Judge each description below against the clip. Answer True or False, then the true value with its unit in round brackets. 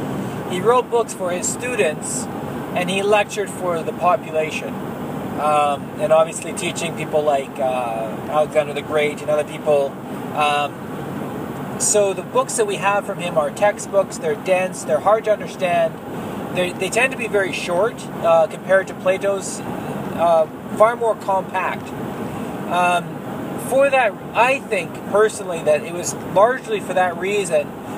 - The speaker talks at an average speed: True (150 wpm)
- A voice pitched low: False (185 Hz)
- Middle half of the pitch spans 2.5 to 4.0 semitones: False (5.2 semitones)